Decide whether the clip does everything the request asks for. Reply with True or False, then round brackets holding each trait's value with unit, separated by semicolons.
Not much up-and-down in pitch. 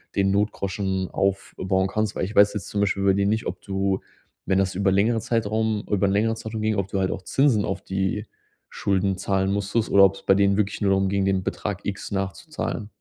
True (1.4 semitones)